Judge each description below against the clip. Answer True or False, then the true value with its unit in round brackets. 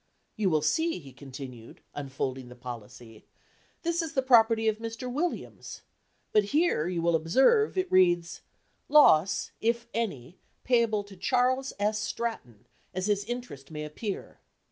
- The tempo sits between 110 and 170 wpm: True (145 wpm)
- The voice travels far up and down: True (8.7 semitones)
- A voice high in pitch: True (205 Hz)